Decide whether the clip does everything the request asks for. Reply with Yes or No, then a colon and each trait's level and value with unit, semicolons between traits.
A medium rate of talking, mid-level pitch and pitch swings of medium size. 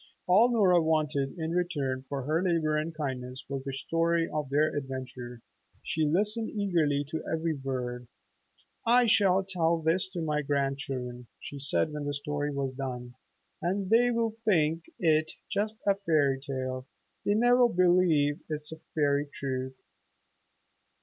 Yes: average, 145 wpm; medium, 155 Hz; average, 4.6 semitones